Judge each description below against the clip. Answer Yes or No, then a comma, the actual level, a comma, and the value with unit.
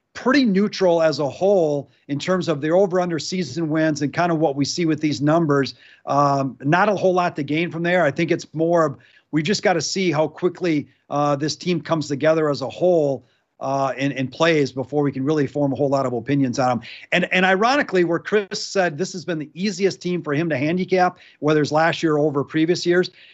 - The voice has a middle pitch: Yes, medium, 160 Hz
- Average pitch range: Yes, average, 3.9 semitones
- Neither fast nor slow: No, fast, 230 wpm